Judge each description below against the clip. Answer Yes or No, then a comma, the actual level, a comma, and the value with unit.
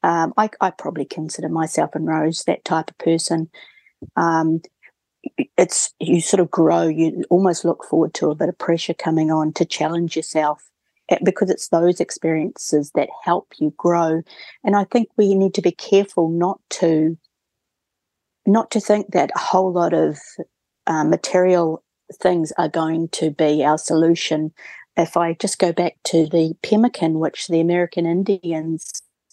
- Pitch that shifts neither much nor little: No, narrow, 2.2 semitones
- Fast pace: No, average, 160 wpm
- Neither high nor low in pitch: Yes, medium, 170 Hz